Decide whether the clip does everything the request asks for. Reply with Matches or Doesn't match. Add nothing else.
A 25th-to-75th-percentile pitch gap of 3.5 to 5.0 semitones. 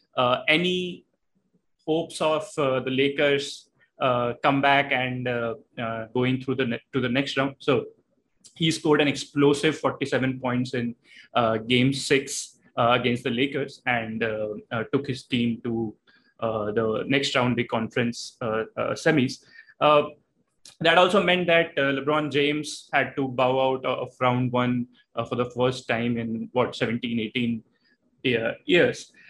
Doesn't match